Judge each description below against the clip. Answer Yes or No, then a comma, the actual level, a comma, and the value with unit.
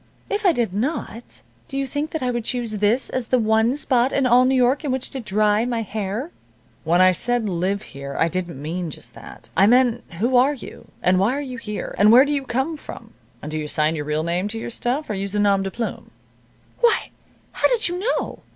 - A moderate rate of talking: No, fast, 235 wpm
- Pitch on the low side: No, high, 230 Hz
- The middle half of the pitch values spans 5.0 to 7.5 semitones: Yes, average, 5.3 semitones